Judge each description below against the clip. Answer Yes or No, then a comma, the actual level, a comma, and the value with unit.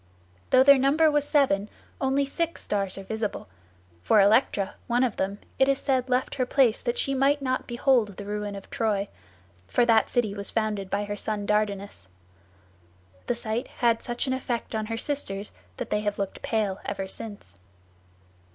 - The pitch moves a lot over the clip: No, average, 4.3 semitones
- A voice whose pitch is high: Yes, high, 220 Hz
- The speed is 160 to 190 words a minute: Yes, average, 180 wpm